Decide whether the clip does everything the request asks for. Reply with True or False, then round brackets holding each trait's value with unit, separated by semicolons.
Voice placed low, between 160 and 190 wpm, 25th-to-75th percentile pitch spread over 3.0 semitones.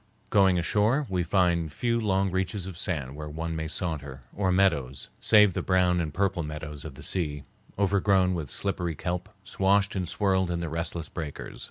True (90 Hz; 180 wpm; 3.5 semitones)